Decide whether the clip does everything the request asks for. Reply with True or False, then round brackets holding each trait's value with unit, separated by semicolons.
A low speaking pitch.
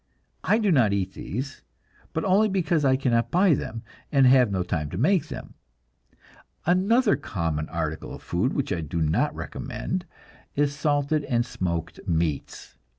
True (130 Hz)